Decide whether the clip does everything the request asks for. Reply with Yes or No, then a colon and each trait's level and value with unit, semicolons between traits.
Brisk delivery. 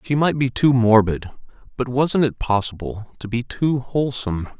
No: average, 170 wpm